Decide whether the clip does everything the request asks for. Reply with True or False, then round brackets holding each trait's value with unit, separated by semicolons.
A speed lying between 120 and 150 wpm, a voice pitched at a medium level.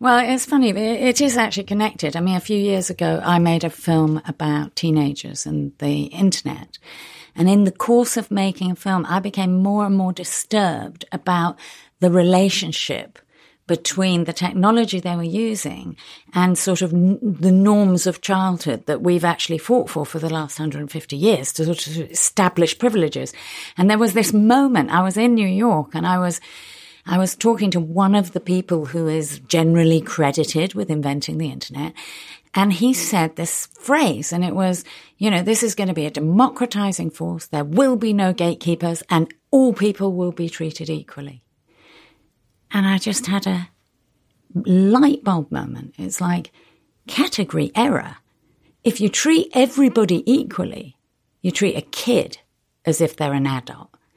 False (170 wpm; 180 Hz)